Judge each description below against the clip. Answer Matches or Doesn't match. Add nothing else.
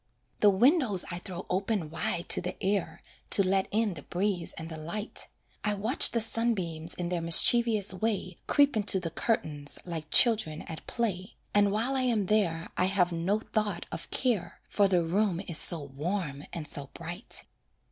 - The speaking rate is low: Doesn't match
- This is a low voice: Doesn't match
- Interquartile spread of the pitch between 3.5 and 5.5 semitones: Matches